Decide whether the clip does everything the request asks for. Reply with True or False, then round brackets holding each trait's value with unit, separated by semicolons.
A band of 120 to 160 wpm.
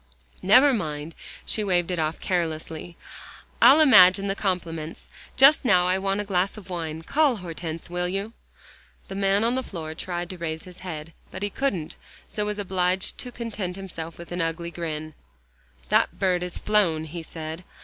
False (175 wpm)